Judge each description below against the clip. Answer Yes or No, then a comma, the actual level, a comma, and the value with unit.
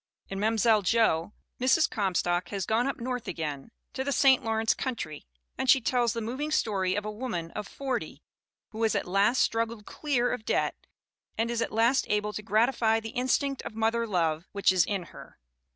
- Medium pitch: No, high, 225 Hz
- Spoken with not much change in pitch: No, average, 3.6 semitones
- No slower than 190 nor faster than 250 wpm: Yes, average, 195 wpm